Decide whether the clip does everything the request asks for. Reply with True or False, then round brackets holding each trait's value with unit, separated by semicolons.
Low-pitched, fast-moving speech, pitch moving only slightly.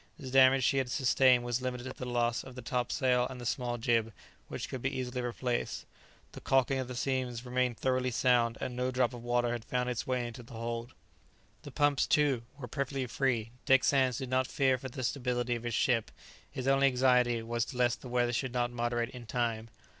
True (125 Hz; 215 wpm; 1.4 semitones)